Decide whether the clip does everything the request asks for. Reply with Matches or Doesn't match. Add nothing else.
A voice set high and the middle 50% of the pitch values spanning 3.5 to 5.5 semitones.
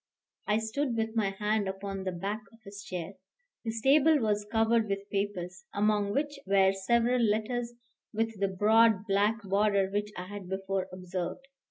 Doesn't match